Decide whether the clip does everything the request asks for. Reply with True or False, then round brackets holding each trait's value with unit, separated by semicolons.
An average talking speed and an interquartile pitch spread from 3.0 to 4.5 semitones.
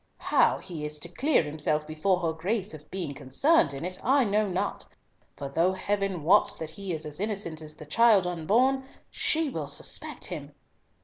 False (185 wpm; 5.0 semitones)